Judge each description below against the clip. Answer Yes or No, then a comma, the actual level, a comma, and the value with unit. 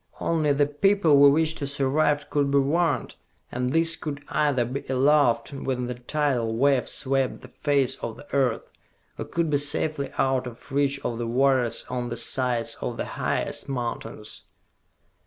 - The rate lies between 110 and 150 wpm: No, average, 170 wpm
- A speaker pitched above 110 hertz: Yes, medium, 140 Hz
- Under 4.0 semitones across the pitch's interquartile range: Yes, average, 2.7 semitones